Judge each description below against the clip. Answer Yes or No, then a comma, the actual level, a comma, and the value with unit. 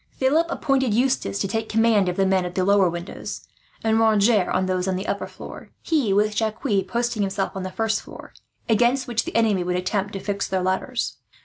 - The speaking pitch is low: No, high, 205 Hz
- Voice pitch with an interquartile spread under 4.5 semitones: Yes, average, 3.4 semitones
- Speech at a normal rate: No, fast, 215 wpm